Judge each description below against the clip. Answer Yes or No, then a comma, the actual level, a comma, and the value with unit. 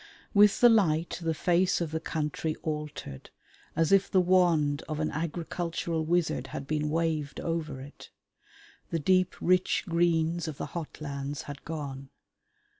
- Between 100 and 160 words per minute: Yes, average, 150 wpm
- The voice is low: No, medium, 160 Hz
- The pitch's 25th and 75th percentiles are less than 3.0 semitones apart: Yes, narrow, 2.5 semitones